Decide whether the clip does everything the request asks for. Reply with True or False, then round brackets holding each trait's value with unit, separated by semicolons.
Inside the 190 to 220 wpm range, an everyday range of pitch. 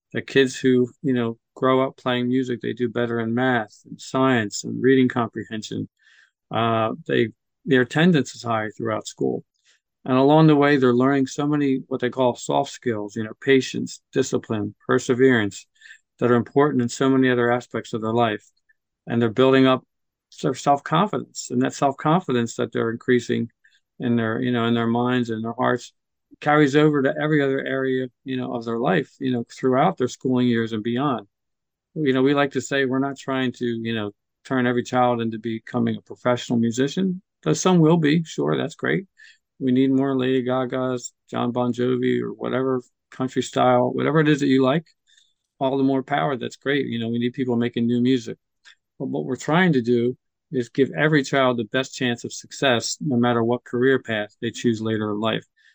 False (195 wpm; 2.1 semitones)